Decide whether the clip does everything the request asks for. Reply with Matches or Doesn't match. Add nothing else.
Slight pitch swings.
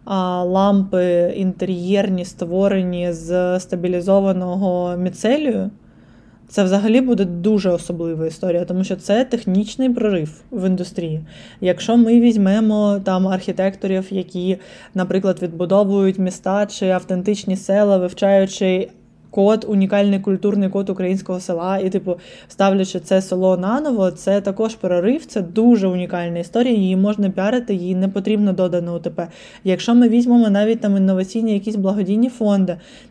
Matches